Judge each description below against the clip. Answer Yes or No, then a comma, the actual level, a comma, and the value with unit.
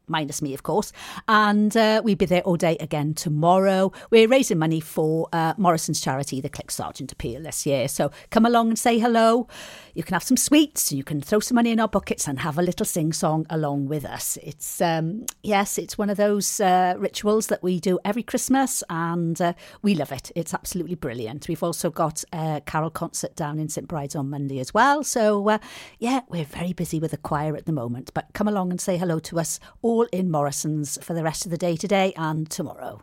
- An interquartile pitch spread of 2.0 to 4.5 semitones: No, average, 4.9 semitones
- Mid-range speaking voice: Yes, medium, 175 Hz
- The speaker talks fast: Yes, fast, 220 wpm